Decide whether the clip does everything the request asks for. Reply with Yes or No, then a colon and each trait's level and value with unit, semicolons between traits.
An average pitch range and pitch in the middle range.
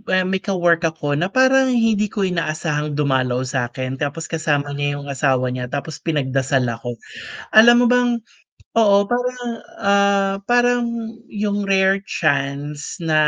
No: wide, 6.3 semitones; medium, 165 Hz